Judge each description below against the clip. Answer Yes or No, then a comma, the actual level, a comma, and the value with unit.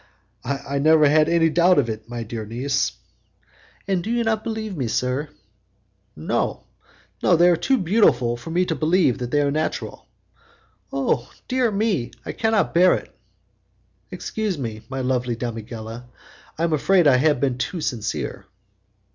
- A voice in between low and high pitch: Yes, medium, 145 Hz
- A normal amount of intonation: No, wide, 6.6 semitones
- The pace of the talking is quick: No, average, 150 wpm